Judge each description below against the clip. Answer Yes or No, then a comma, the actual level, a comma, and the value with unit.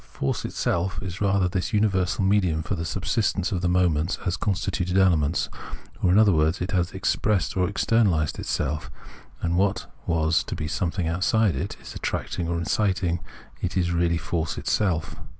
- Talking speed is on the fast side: No, average, 170 wpm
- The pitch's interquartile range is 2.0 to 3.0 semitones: Yes, narrow, 2.6 semitones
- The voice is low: Yes, very low, 90 Hz